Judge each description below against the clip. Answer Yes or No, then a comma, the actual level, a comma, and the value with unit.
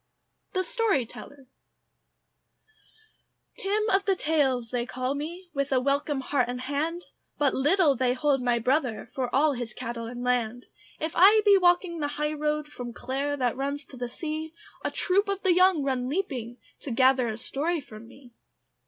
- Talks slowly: No, average, 170 wpm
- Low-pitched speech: No, very high, 280 Hz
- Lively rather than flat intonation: No, average, 4.8 semitones